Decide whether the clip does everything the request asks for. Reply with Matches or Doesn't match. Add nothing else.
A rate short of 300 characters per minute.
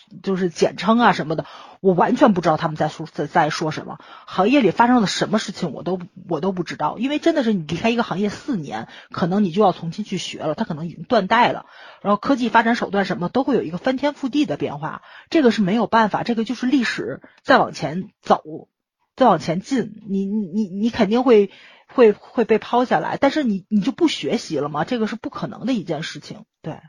Doesn't match